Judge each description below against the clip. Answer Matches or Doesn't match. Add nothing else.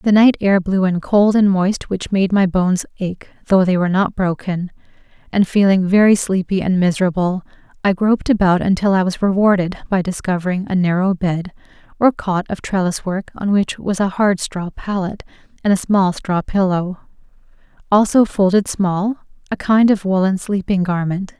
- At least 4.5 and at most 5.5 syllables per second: Matches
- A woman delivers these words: Matches